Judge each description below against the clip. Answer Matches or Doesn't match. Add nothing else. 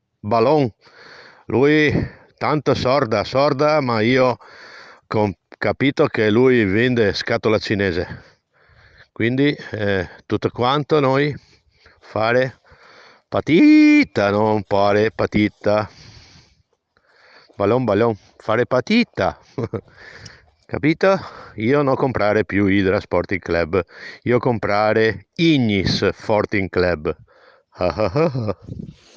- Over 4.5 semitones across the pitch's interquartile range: Matches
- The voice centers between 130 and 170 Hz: Doesn't match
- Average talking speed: Doesn't match